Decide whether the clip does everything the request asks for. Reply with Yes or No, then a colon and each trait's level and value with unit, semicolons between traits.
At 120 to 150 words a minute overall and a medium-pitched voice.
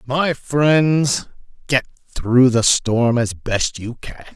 No: average, 140 wpm; low, 125 Hz